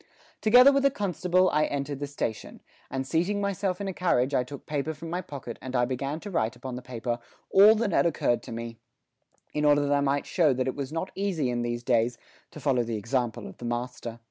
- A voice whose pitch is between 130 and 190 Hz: Yes, medium, 140 Hz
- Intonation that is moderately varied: No, wide, 6.5 semitones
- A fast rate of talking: Yes, fast, 230 wpm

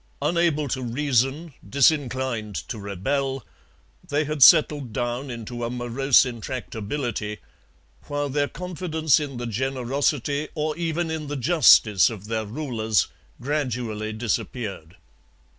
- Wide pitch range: No, average, 4.2 semitones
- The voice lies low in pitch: Yes, low, 130 Hz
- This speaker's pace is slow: Yes, slow, 115 wpm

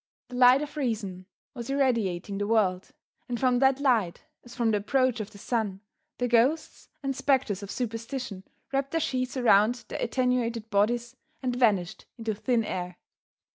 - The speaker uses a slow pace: No, average, 165 wpm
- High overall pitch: Yes, high, 235 Hz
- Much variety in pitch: No, average, 3.6 semitones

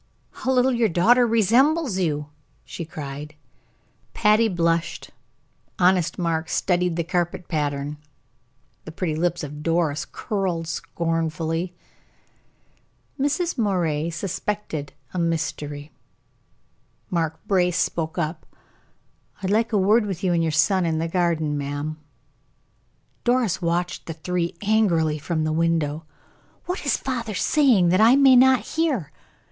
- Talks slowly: Yes, slow, 125 wpm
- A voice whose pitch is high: No, medium, 175 Hz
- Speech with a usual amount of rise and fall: Yes, average, 4.8 semitones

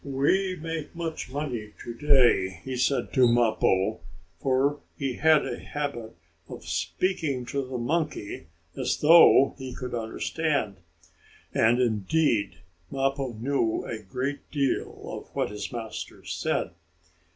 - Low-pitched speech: Yes, low, 130 Hz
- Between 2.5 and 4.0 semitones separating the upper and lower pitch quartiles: No, average, 4.6 semitones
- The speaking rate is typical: No, slow, 130 wpm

